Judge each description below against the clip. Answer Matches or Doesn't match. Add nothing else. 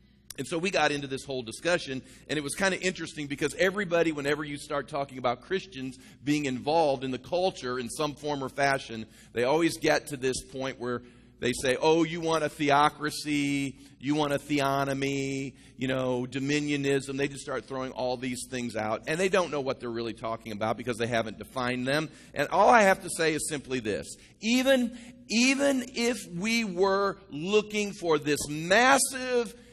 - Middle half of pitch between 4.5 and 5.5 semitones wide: Matches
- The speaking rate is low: Doesn't match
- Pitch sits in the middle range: Matches